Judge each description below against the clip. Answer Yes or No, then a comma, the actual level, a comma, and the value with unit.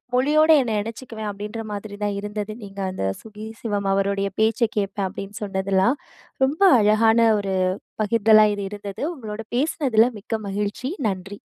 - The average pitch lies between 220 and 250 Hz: No, high, 210 Hz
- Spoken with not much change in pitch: Yes, narrow, 2.2 semitones